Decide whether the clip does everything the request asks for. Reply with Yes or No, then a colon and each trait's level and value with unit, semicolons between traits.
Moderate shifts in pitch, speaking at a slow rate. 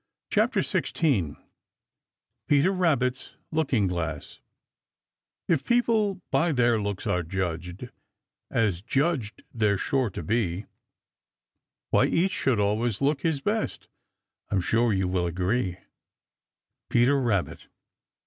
No: wide, 7.1 semitones; slow, 110 wpm